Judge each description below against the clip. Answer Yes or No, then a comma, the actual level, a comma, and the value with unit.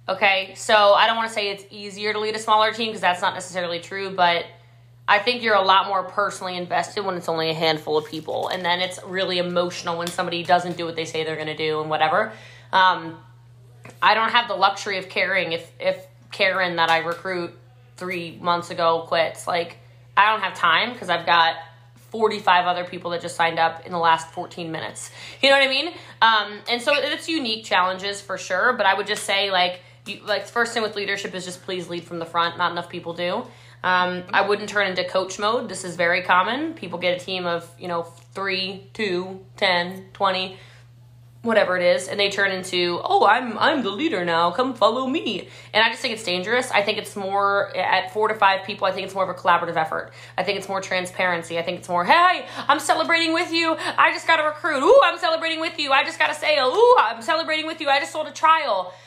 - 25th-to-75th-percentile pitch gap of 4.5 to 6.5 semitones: No, average, 3.8 semitones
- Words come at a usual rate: No, fast, 230 wpm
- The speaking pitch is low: No, medium, 185 Hz